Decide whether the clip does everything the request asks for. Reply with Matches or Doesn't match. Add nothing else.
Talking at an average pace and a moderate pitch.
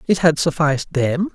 Matches